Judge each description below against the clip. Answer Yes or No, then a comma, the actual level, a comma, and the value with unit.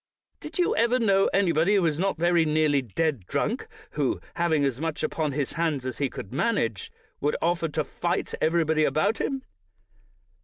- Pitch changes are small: No, average, 3.3 semitones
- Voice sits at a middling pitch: Yes, medium, 160 Hz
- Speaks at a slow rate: No, average, 170 wpm